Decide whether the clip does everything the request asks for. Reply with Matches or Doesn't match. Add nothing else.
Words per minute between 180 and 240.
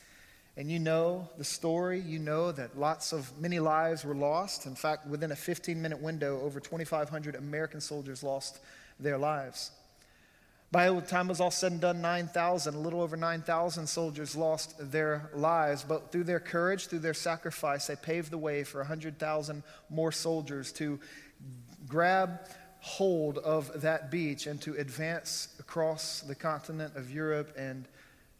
Doesn't match